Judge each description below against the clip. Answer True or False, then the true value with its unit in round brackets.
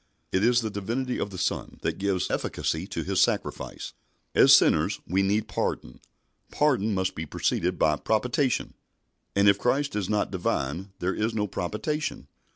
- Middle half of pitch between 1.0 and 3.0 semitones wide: False (4.1 semitones)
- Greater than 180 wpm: False (165 wpm)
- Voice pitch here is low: True (100 Hz)